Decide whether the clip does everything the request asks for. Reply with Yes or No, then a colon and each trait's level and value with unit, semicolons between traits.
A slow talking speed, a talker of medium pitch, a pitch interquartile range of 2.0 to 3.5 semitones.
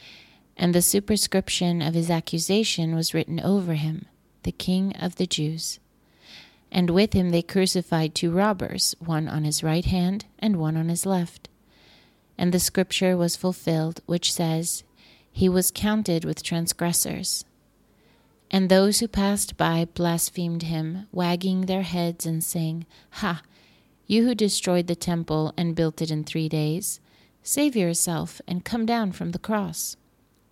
No: average, 150 wpm; medium, 175 Hz; narrow, 2.6 semitones